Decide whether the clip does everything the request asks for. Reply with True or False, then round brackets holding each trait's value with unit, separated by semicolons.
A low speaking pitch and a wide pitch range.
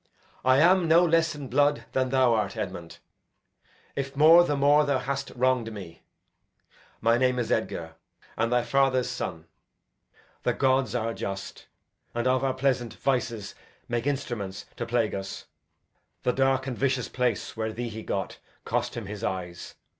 False (125 Hz; 3.5 semitones)